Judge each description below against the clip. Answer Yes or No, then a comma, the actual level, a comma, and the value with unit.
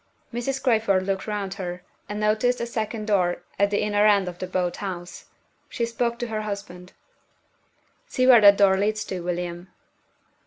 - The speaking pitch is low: No, high, 205 Hz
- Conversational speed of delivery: Yes, average, 170 wpm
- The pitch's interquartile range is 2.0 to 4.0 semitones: Yes, average, 3.0 semitones